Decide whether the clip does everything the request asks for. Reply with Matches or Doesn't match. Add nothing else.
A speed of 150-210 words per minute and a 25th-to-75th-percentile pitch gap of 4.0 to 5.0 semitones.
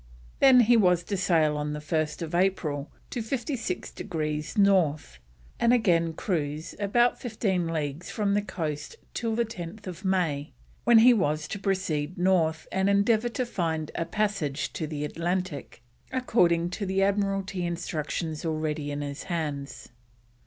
Doesn't match